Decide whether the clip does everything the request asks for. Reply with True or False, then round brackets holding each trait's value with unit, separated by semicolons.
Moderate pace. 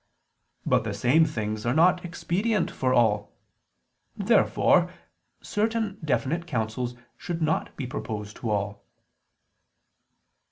False (110 wpm)